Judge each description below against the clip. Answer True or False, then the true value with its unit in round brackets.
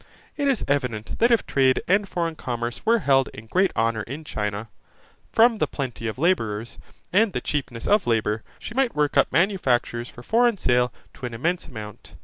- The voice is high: False (135 Hz)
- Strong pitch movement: True (8.9 semitones)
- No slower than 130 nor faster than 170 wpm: False (185 wpm)